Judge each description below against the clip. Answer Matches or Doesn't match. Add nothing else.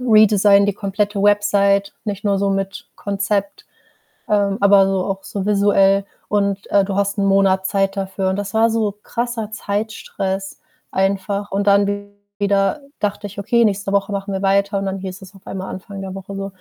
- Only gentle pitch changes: Matches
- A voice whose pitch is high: Matches